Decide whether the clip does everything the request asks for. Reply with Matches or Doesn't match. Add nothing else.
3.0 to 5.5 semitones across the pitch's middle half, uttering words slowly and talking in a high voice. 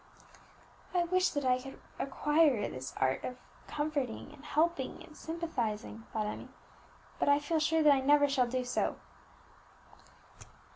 Doesn't match